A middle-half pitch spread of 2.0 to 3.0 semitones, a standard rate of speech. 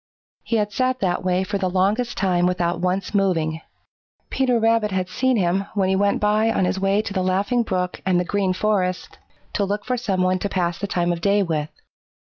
No: narrow, 2.4 semitones; fast, 215 wpm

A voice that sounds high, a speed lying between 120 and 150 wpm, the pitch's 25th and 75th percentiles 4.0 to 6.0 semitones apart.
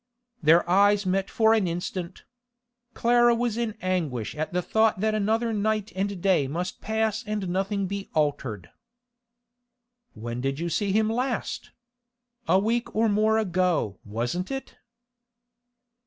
Yes: high, 195 Hz; average, 140 wpm; average, 4.3 semitones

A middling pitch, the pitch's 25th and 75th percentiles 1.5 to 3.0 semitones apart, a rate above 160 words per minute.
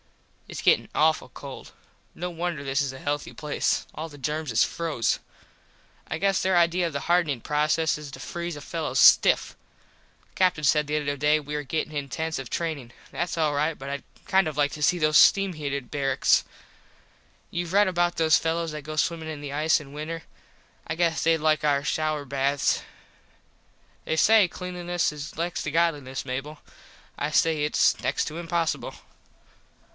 Yes: medium, 155 Hz; average, 2.7 semitones; average, 180 wpm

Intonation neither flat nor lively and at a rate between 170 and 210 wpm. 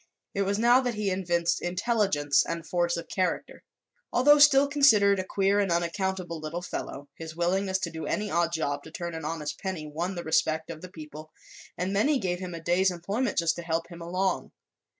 Yes: average, 3.1 semitones; average, 200 wpm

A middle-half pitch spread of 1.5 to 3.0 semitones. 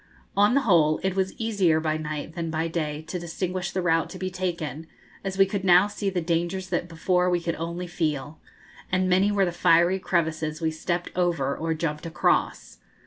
Yes: narrow, 2.5 semitones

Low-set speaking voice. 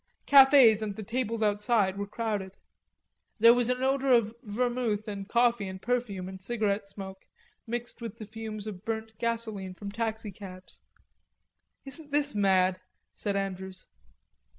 No: high, 215 Hz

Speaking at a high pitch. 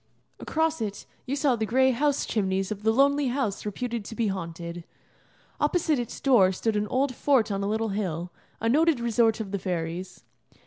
Yes: high, 225 Hz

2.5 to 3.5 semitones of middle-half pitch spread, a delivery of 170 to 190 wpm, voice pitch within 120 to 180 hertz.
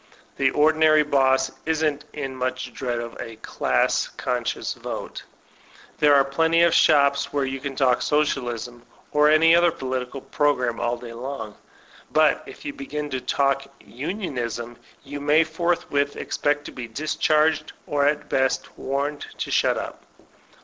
No: average, 3.0 semitones; average, 150 wpm; medium, 140 Hz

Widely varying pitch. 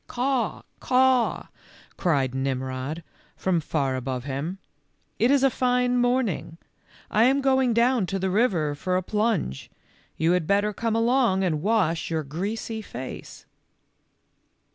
Yes: wide, 7.8 semitones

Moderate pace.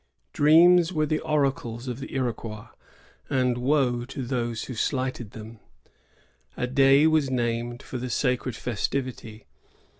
No: slow, 130 wpm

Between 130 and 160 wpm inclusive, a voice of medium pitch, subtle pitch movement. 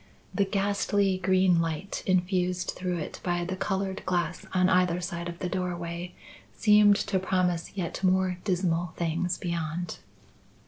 Yes: average, 140 wpm; medium, 180 Hz; narrow, 1.5 semitones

